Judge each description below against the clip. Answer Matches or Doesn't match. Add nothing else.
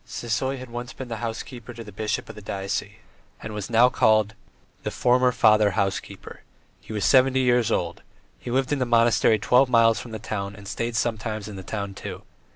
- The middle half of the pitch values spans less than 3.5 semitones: Matches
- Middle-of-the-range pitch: Doesn't match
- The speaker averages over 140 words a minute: Matches